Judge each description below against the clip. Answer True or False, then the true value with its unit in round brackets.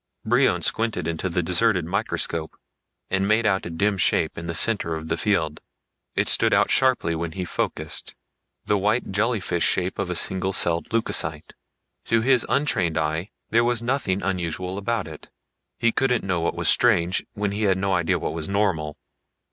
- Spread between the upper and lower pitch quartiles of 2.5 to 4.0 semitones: False (4.7 semitones)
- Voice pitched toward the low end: True (95 Hz)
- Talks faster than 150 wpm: True (180 wpm)